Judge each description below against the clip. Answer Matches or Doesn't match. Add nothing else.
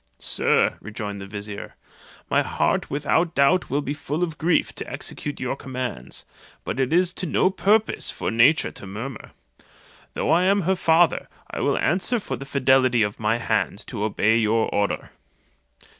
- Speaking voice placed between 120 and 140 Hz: Matches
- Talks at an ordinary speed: Matches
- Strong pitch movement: Matches